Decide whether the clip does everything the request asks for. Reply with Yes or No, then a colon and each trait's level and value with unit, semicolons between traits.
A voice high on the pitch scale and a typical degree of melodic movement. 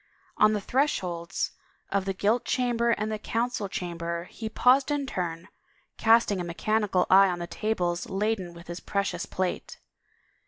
Yes: high, 200 Hz; average, 4.1 semitones